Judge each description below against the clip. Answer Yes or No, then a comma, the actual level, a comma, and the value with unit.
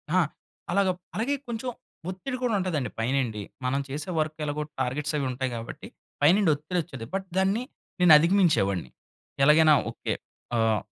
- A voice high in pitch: No, medium, 155 Hz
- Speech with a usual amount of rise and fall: No, wide, 6.3 semitones